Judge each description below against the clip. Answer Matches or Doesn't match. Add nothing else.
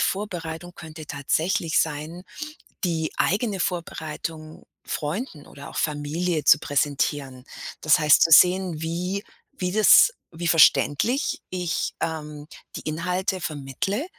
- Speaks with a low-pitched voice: Doesn't match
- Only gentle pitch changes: Doesn't match